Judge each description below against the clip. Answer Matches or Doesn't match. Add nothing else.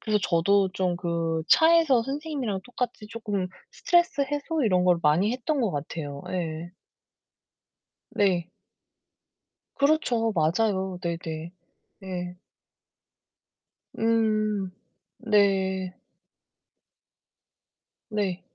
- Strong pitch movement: Doesn't match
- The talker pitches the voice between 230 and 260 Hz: Doesn't match